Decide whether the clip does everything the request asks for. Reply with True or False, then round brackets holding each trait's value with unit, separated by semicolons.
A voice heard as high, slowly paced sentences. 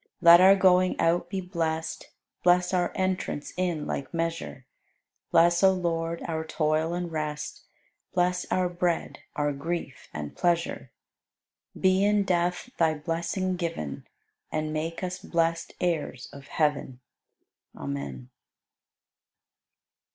False (170 Hz; 120 wpm)